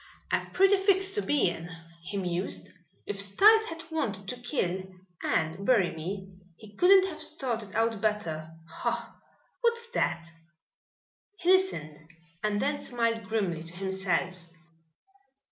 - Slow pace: Yes, slow, 130 wpm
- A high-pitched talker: Yes, high, 210 Hz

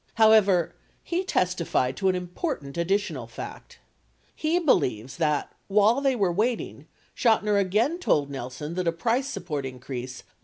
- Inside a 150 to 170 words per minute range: No, average, 140 wpm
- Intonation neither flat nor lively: No, wide, 7.4 semitones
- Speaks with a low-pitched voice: No, medium, 185 Hz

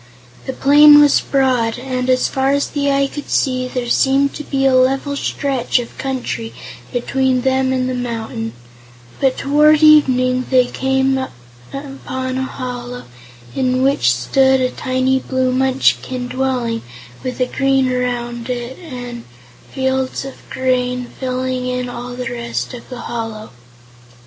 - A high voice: Yes, very high, 255 Hz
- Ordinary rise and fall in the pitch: No, narrow, 1.4 semitones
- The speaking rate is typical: Yes, average, 145 wpm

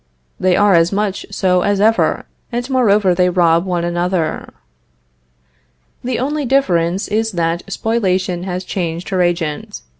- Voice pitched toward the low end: No, medium, 185 Hz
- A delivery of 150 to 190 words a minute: No, average, 140 wpm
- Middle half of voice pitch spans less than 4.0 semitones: Yes, average, 3.3 semitones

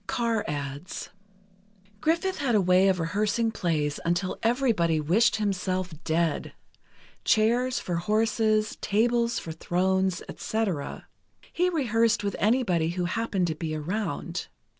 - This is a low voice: No, high, 200 Hz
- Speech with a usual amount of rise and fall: Yes, average, 4.9 semitones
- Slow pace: Yes, slow, 115 wpm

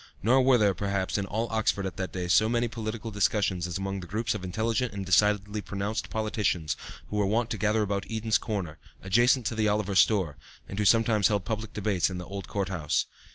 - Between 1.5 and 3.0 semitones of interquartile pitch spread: Yes, narrow, 2.4 semitones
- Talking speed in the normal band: No, fast, 215 wpm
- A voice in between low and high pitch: No, low, 105 Hz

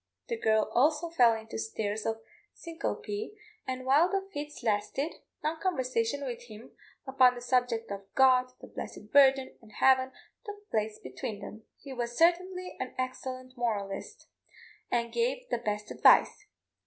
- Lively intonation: Yes, wide, 5.9 semitones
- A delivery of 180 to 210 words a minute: No, average, 150 wpm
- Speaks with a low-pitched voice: No, very high, 255 Hz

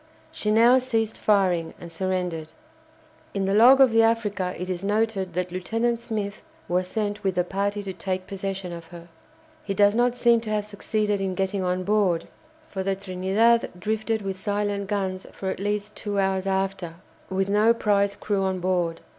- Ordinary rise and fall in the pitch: No, narrow, 2.3 semitones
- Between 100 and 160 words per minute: No, average, 180 wpm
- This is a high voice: Yes, high, 195 Hz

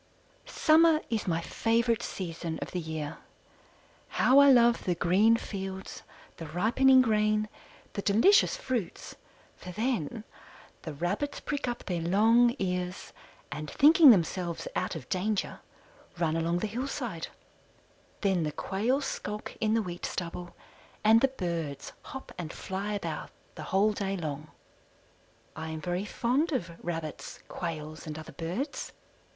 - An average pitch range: No, wide, 5.8 semitones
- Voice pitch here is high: Yes, high, 195 Hz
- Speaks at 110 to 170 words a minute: Yes, average, 140 wpm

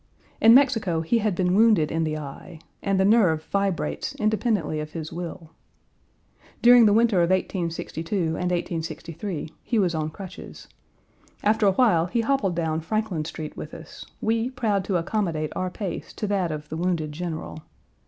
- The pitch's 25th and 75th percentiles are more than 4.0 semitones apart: Yes, average, 4.8 semitones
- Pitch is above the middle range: No, medium, 180 Hz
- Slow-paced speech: No, average, 165 wpm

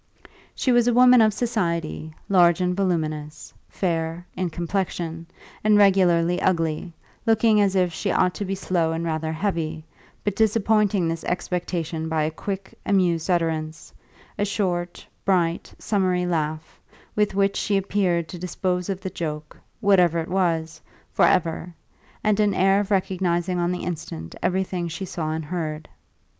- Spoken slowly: No, average, 150 wpm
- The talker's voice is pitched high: No, medium, 180 Hz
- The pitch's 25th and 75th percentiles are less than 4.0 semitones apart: Yes, average, 3.1 semitones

